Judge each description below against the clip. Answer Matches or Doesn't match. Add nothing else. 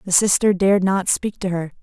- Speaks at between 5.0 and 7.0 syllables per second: Matches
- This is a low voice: Doesn't match